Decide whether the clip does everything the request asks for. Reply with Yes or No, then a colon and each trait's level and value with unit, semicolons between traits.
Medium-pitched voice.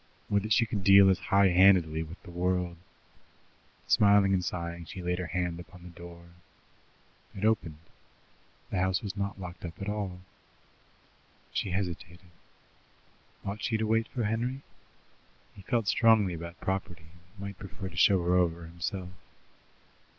No: very low, 95 Hz